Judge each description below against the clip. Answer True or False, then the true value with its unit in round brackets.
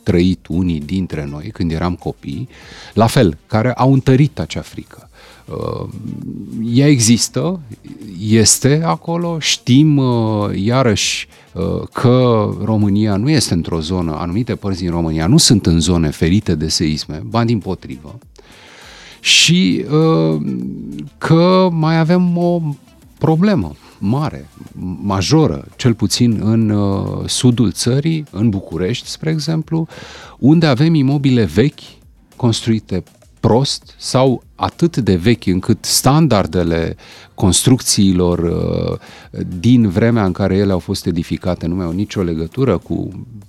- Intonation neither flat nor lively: False (6.6 semitones)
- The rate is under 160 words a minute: True (120 wpm)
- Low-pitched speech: True (110 Hz)